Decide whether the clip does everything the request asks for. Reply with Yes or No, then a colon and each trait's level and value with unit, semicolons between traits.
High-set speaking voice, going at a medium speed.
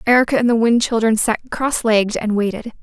No: high, 225 Hz; fast, 210 wpm